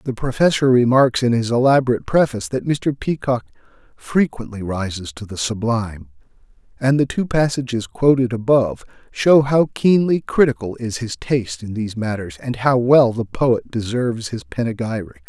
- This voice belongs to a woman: No, male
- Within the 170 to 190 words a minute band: No, average, 155 wpm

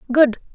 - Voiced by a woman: Yes, female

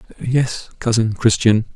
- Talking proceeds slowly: Yes, slow, 105 wpm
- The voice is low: Yes, low, 115 Hz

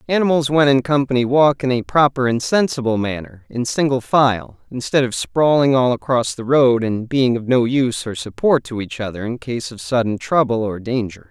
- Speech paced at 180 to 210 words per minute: Yes, average, 200 wpm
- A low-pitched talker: Yes, low, 125 Hz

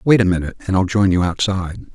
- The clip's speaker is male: Yes, male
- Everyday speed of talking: No, fast, 245 wpm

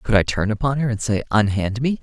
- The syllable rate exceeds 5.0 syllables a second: Yes, 6.0 syllables/s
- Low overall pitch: Yes, low, 115 Hz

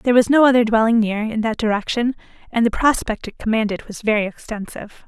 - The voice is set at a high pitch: Yes, high, 225 Hz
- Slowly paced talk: No, average, 200 wpm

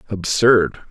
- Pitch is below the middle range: Yes, low, 105 Hz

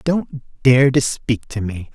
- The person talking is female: No, male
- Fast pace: No, average, 185 wpm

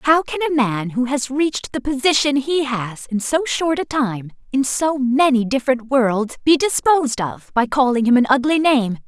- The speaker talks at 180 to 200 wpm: Yes, average, 185 wpm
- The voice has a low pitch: No, very high, 260 Hz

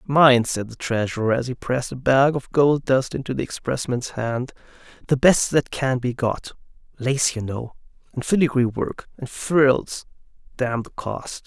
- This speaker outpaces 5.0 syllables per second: No, 4.5 syllables/s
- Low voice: Yes, low, 130 Hz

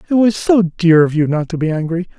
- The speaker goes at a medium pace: No, fast, 275 wpm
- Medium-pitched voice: Yes, medium, 175 Hz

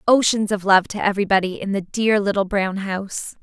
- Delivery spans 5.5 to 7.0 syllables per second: Yes, 5.6 syllables/s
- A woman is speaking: Yes, female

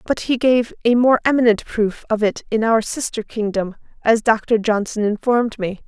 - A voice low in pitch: No, high, 225 Hz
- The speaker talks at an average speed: Yes, average, 185 wpm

